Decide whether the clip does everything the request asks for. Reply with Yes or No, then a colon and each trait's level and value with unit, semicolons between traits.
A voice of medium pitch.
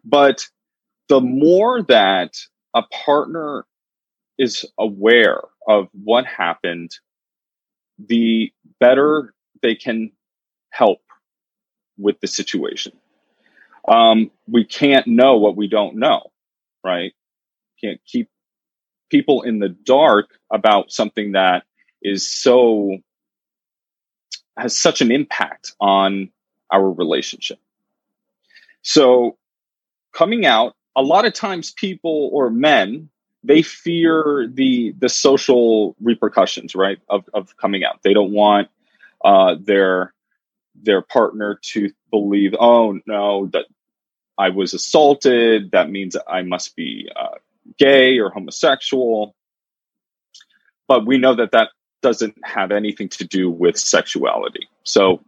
No: low, 115 Hz